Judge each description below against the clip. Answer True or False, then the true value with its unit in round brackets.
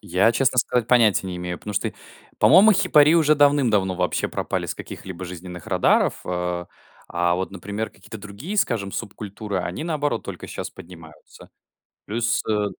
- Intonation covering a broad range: True (5.7 semitones)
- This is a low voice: True (105 Hz)